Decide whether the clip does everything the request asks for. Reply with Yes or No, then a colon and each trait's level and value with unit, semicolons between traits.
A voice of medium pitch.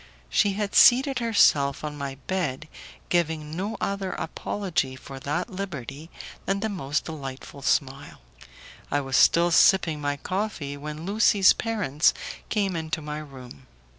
Yes: medium, 160 Hz